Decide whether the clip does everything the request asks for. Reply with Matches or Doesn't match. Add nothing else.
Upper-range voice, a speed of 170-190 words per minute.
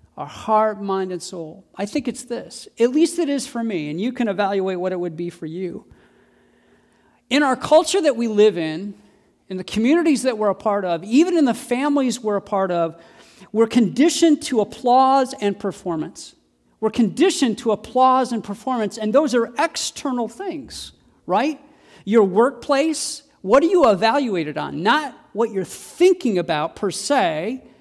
Matches